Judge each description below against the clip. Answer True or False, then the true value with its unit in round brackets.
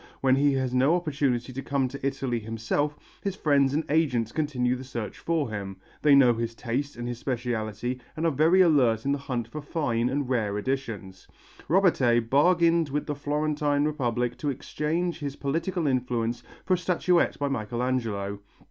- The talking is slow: False (175 wpm)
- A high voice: False (135 Hz)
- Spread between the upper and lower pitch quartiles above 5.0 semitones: False (3.8 semitones)